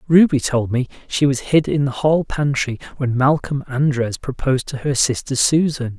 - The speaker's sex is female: No, male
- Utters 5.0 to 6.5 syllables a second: No, 4.8 syllables/s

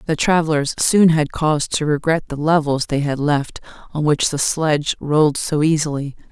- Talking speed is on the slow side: No, average, 180 wpm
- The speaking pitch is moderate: Yes, medium, 150 Hz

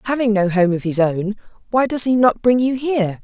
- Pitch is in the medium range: No, high, 220 Hz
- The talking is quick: Yes, fast, 240 wpm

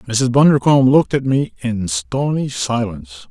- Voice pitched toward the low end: Yes, low, 125 Hz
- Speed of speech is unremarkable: Yes, average, 145 wpm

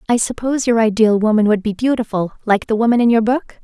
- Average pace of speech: No, fast, 230 wpm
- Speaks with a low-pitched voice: No, high, 225 Hz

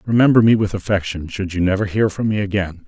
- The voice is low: Yes, low, 100 Hz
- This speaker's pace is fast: Yes, fast, 230 wpm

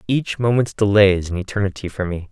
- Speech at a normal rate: No, fast, 210 wpm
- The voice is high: No, low, 100 Hz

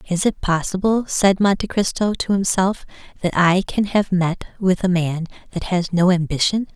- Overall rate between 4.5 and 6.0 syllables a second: Yes, 4.8 syllables/s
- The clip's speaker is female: Yes, female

